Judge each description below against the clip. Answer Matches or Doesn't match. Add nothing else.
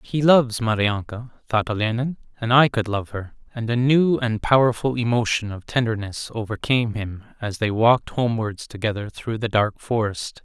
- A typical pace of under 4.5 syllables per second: Doesn't match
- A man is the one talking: Matches